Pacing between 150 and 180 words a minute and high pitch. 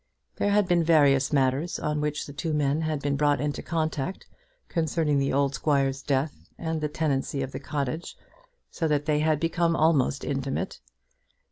No: average, 170 wpm; medium, 150 Hz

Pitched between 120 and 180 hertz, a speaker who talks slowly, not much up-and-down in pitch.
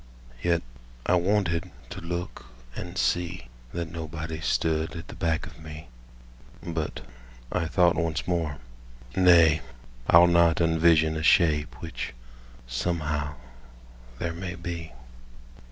No: very low, 85 Hz; slow, 120 wpm; narrow, 1.7 semitones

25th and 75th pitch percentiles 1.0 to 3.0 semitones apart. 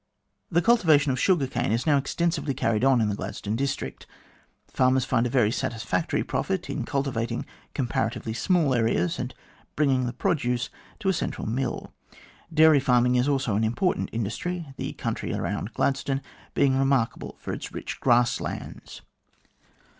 No: average, 3.7 semitones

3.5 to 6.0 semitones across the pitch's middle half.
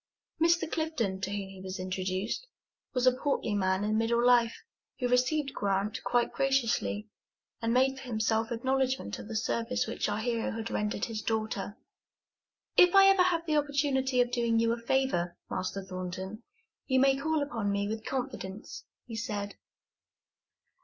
Yes: average, 4.5 semitones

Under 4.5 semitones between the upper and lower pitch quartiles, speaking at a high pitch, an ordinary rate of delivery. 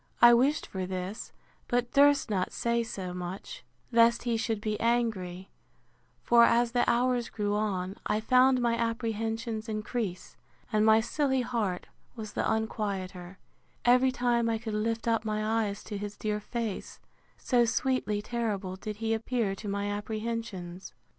Yes: narrow, 2.6 semitones; high, 220 Hz; average, 155 wpm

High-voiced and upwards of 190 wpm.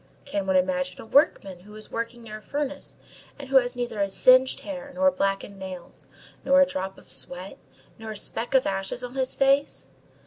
Yes: high, 230 Hz; average, 200 wpm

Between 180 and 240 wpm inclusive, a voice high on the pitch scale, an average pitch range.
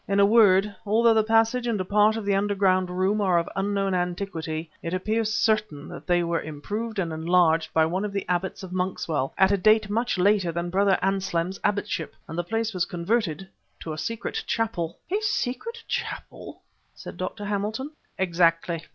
Yes: average, 185 wpm; high, 195 Hz; average, 3.6 semitones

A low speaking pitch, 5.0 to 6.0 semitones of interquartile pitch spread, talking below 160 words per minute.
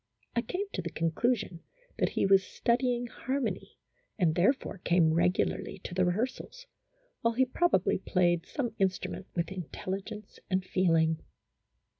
No: high, 190 Hz; wide, 5.4 semitones; average, 145 wpm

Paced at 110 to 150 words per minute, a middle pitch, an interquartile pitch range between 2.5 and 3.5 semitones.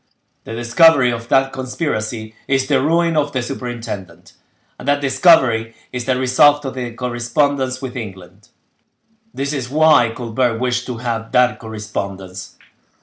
No: average, 145 wpm; low, 125 Hz; average, 3.2 semitones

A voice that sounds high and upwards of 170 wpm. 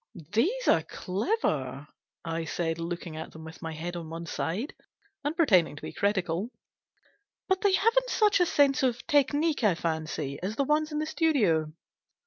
Yes: high, 200 Hz; average, 180 wpm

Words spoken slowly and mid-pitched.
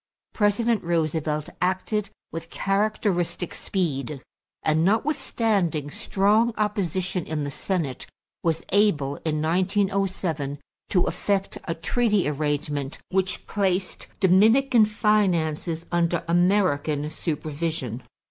Yes: slow, 95 wpm; medium, 175 Hz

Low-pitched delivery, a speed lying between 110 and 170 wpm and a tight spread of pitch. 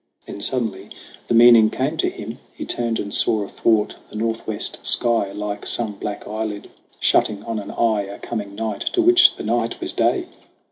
No: low, 110 Hz; average, 180 wpm; narrow, 2.2 semitones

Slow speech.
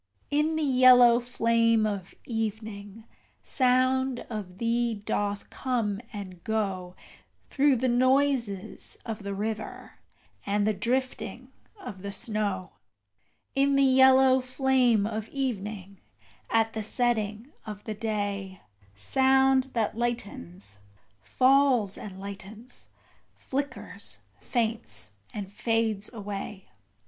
Yes: slow, 105 wpm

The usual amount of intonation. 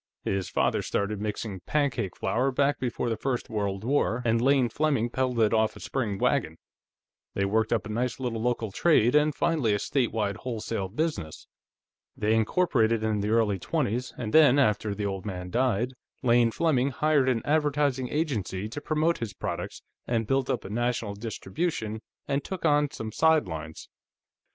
Yes: average, 4.6 semitones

